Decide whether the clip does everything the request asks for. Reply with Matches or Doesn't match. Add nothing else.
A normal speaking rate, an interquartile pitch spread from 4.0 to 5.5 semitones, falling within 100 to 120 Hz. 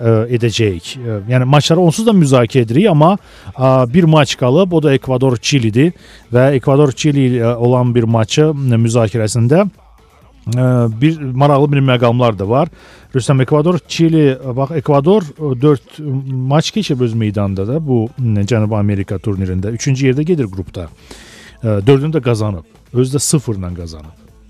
Doesn't match